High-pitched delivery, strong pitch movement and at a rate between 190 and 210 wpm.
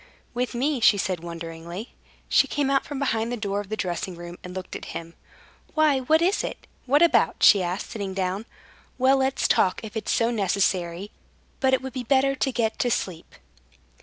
Yes: high, 220 Hz; wide, 6.2 semitones; average, 195 wpm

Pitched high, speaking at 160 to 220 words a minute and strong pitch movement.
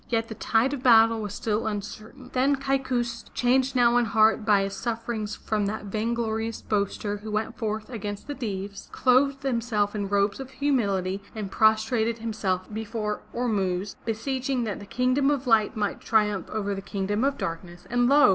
No: high, 220 Hz; average, 175 wpm; average, 3.1 semitones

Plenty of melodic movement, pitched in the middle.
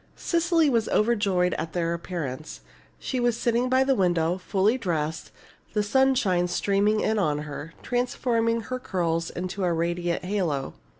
No: wide, 5.8 semitones; high, 195 Hz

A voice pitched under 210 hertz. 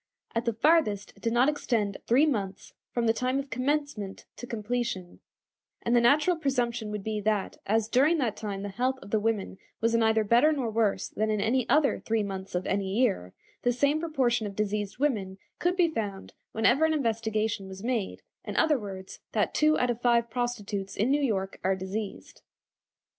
No: high, 225 Hz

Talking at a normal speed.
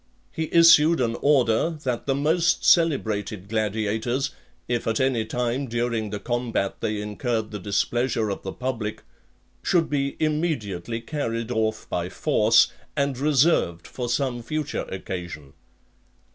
No: slow, 130 wpm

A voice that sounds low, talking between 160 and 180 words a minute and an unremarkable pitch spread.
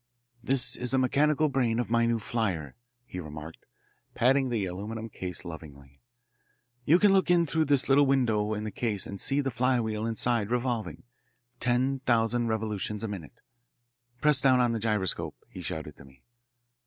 Yes: low, 115 Hz; average, 165 wpm; average, 4.5 semitones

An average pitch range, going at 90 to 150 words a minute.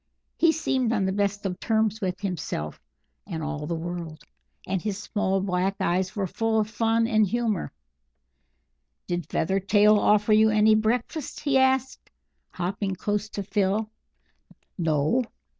Yes: average, 3.2 semitones; average, 140 wpm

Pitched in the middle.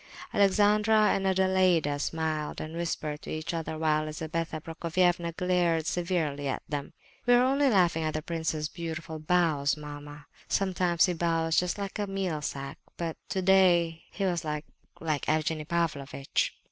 Yes: medium, 165 Hz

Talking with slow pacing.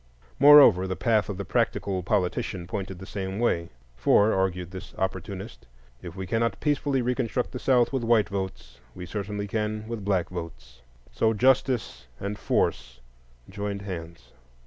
No: average, 150 wpm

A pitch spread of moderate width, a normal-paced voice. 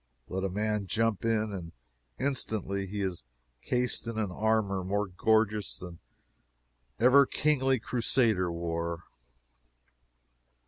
No: average, 3.5 semitones; slow, 110 wpm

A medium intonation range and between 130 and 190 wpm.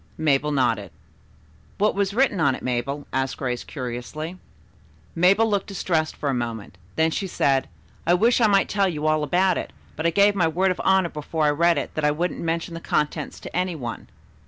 No: average, 4.9 semitones; fast, 205 wpm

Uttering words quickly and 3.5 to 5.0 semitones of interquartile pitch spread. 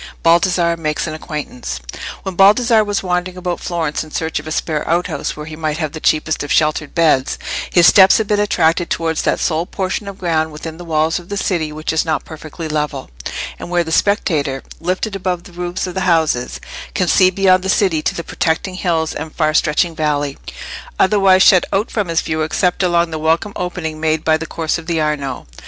No: fast, 210 wpm; average, 2.8 semitones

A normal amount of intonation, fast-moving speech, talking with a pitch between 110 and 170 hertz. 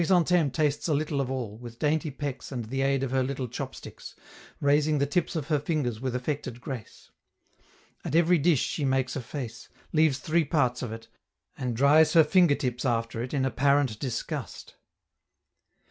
No: average, 3.4 semitones; average, 175 wpm; medium, 140 Hz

